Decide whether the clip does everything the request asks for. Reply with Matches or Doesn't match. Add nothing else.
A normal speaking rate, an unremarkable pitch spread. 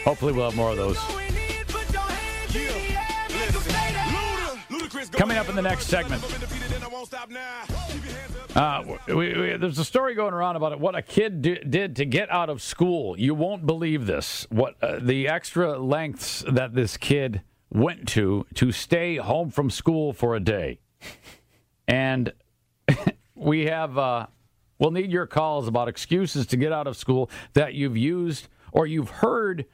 Doesn't match